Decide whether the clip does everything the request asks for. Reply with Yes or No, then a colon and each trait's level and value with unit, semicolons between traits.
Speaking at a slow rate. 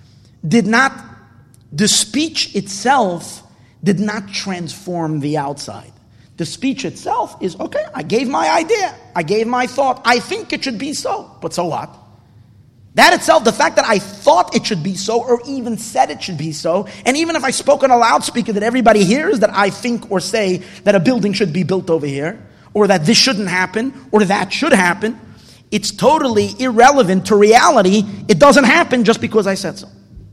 No: average, 190 wpm